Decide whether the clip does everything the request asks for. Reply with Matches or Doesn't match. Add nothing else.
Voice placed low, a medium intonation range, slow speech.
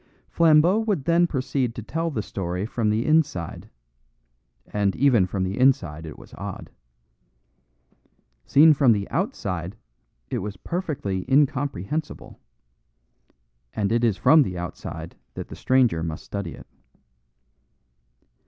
Doesn't match